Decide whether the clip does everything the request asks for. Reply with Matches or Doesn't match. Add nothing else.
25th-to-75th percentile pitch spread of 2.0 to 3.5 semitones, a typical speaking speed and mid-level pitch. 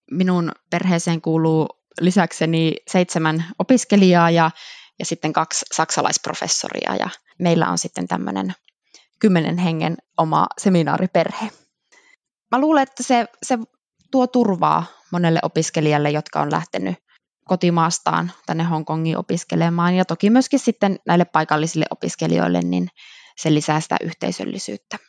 Doesn't match